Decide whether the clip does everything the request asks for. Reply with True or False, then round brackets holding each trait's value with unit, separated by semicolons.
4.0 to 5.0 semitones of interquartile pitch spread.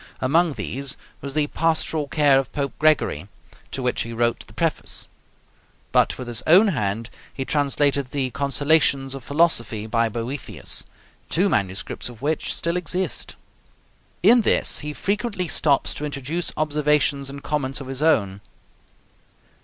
False (3.4 semitones)